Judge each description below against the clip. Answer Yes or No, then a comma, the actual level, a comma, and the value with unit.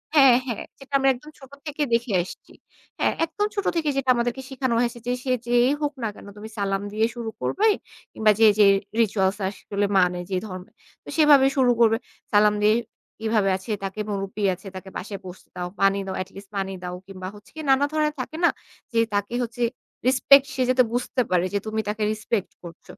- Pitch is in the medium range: No, high, 220 Hz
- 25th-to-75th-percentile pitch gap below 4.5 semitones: No, average, 5.0 semitones